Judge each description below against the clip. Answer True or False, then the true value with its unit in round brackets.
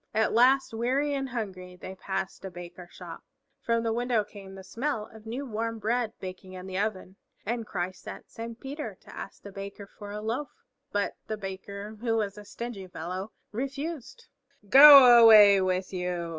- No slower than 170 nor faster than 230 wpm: True (180 wpm)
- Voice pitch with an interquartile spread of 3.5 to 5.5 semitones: True (3.8 semitones)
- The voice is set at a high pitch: True (210 Hz)